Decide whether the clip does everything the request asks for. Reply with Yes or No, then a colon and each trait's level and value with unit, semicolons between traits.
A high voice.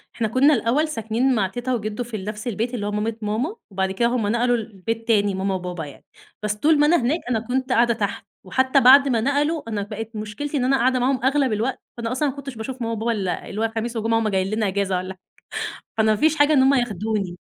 Yes: high, 230 Hz